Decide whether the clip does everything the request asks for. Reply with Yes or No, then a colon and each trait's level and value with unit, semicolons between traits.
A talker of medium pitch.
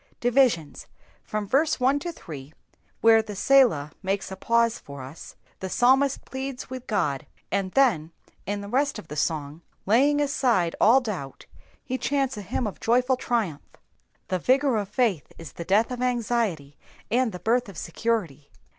No: high, 220 Hz